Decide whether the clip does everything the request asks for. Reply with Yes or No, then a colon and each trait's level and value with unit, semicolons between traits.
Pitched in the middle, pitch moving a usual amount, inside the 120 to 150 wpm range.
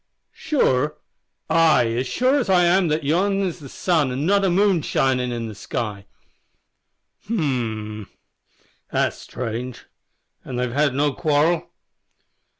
No: medium, 145 Hz; wide, 6.0 semitones; average, 140 wpm